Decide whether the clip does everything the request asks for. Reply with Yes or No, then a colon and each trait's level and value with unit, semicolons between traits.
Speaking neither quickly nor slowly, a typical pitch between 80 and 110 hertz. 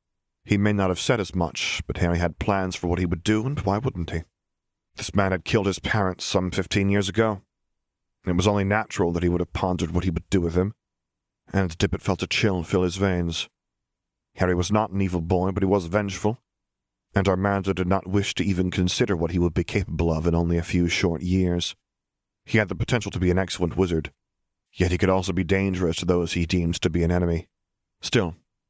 No: fast, 225 wpm; very low, 95 Hz